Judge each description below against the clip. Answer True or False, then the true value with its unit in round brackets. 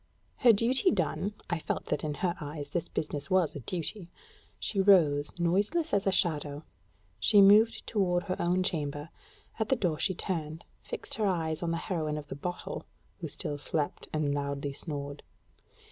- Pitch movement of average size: True (4.7 semitones)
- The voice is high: False (170 Hz)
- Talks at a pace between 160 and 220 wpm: True (175 wpm)